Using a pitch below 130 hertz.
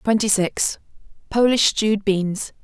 No: high, 210 Hz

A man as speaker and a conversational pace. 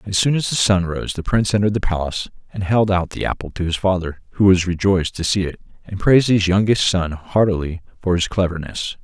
No: male; fast, 225 wpm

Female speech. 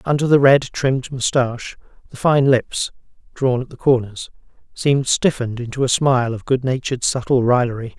No: male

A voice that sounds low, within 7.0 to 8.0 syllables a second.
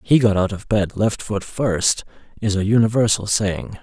No: low, 105 Hz; 4.5 syllables/s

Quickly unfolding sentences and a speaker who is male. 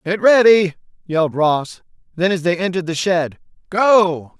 No: average, 150 wpm; male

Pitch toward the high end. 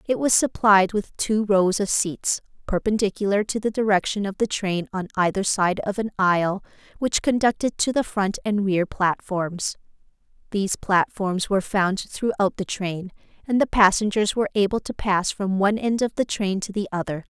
Yes: high, 200 Hz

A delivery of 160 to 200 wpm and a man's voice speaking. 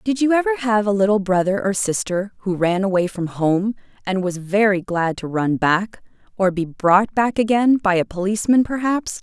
No: average, 195 wpm; female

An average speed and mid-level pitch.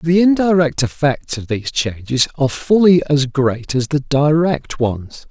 Yes: average, 160 wpm; medium, 145 Hz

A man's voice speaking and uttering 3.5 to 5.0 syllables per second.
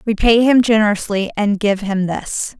No: female; 4.6 syllables/s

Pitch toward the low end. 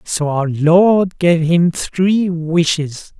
No: medium, 170 Hz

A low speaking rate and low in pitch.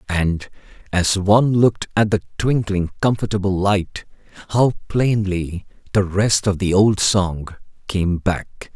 Yes: slow, 130 wpm; low, 100 Hz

